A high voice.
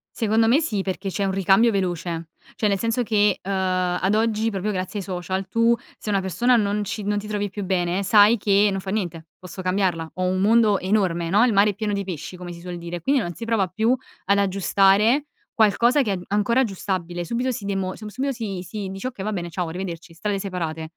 Yes: high, 195 Hz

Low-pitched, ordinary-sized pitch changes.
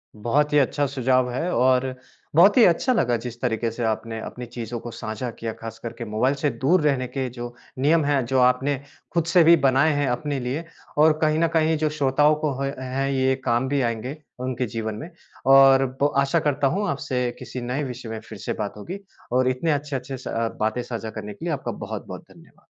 Yes: low, 130 Hz; average, 3.5 semitones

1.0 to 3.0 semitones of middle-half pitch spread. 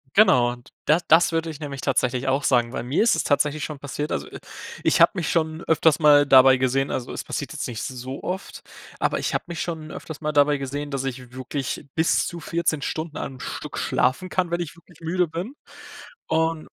No: average, 3.7 semitones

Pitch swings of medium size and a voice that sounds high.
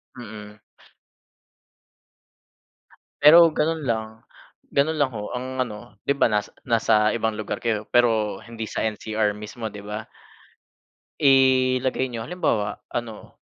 No: average, 3.5 semitones; low, 115 Hz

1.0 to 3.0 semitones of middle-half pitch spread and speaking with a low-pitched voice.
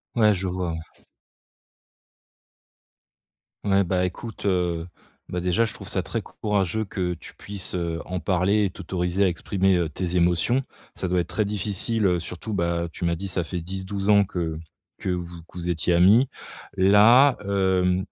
Yes: narrow, 2.4 semitones; very low, 90 Hz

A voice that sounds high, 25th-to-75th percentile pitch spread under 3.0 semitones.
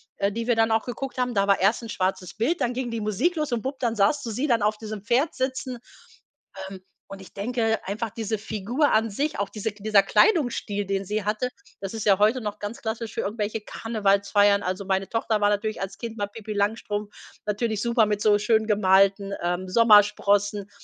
Yes: high, 215 Hz; narrow, 2.4 semitones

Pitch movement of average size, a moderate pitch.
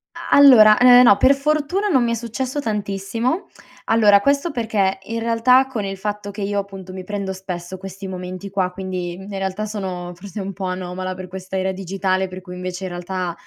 No: average, 3.5 semitones; high, 195 Hz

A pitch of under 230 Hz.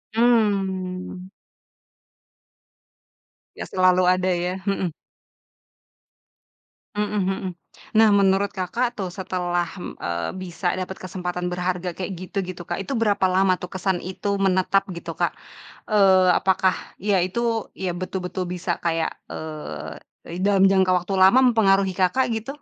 Yes: medium, 185 Hz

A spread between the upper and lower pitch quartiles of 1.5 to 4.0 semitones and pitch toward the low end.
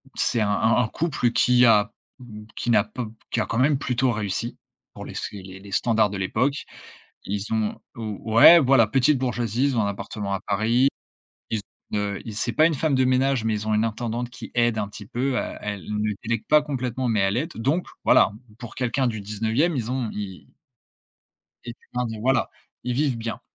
Yes: average, 3.2 semitones; low, 115 Hz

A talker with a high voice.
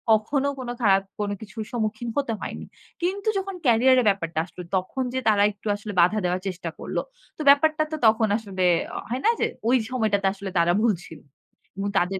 Yes: high, 215 Hz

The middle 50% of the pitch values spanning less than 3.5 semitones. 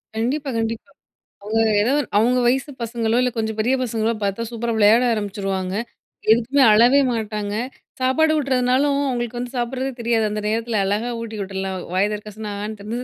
Yes: average, 2.9 semitones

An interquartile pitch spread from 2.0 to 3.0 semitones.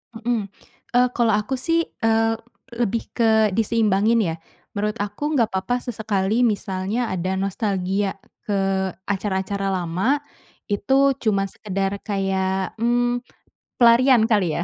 No: average, 3.4 semitones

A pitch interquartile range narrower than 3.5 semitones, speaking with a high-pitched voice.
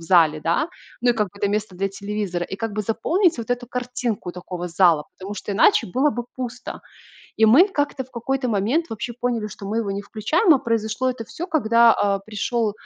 No: average, 3.9 semitones; high, 220 Hz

